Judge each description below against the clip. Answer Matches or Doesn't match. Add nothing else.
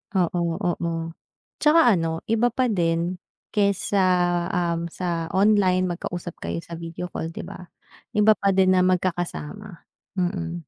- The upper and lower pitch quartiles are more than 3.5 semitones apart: Doesn't match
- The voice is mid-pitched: Matches